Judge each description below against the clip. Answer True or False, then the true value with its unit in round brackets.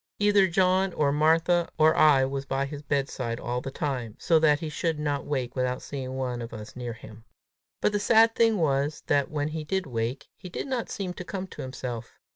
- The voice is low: False (145 Hz)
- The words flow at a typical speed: False (215 wpm)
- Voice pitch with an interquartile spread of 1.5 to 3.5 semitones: False (5.2 semitones)